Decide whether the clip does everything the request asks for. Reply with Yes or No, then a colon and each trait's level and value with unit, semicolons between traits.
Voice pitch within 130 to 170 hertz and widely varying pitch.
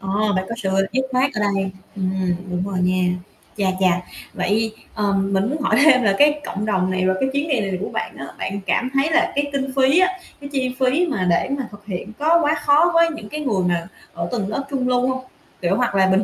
No: high, 215 Hz; wide, 6.1 semitones